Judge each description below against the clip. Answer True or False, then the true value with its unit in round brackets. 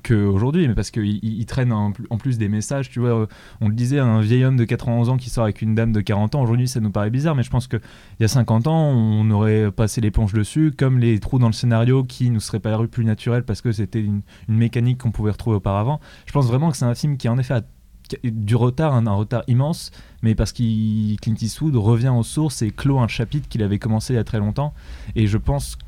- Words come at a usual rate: False (265 wpm)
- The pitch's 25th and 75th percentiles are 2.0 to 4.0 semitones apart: True (2.7 semitones)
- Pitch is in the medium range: False (115 Hz)